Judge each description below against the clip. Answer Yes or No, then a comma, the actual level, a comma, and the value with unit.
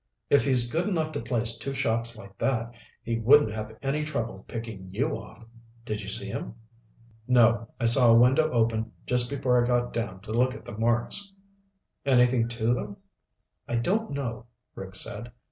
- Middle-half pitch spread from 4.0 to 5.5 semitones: No, average, 2.7 semitones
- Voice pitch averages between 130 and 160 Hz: No, low, 120 Hz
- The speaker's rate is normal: Yes, average, 180 wpm